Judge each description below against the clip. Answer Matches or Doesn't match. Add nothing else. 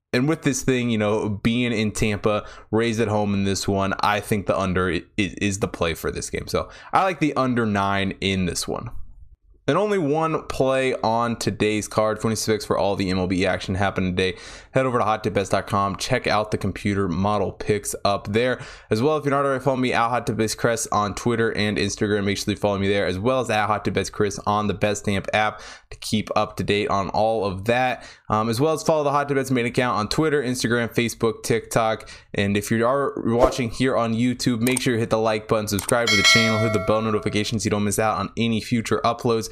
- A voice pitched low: Matches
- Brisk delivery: Matches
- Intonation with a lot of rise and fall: Doesn't match